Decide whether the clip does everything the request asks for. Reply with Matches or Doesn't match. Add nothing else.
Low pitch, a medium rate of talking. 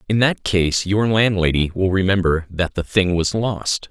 Matches